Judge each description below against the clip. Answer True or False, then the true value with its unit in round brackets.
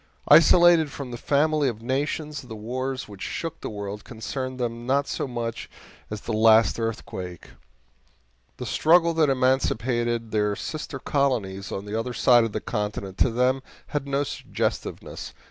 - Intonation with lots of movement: False (4.1 semitones)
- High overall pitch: False (125 Hz)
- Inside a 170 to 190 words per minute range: False (155 wpm)